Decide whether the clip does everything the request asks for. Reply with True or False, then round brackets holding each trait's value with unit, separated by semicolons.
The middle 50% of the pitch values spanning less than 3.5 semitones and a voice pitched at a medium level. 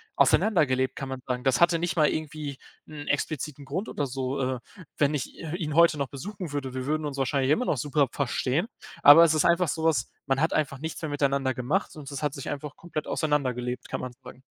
True (2.9 semitones; 145 Hz)